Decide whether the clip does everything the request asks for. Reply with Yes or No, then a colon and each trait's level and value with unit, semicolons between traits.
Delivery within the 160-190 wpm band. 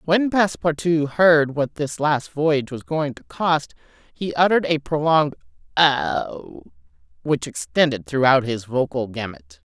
No: slow, 135 wpm